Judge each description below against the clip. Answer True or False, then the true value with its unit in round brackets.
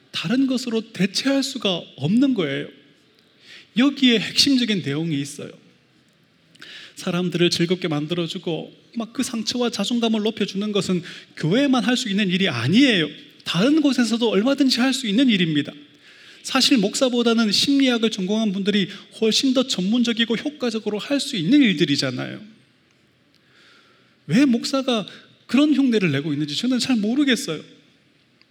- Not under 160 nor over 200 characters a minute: False (310 characters per minute)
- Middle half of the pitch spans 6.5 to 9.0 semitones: False (5.5 semitones)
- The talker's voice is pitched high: True (225 Hz)